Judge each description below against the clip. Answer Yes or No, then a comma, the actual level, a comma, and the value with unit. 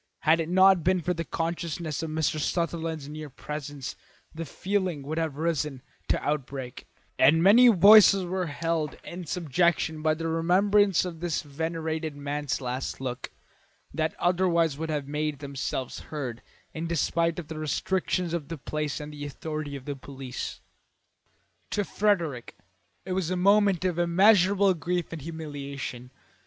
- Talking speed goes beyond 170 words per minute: No, average, 150 wpm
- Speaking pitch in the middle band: Yes, medium, 160 Hz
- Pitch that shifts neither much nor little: Yes, average, 3.3 semitones